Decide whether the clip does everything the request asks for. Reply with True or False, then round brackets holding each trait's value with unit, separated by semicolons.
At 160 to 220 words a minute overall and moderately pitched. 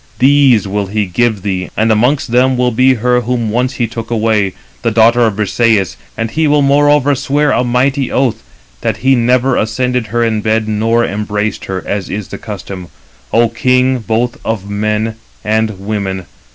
False (175 wpm; 115 Hz)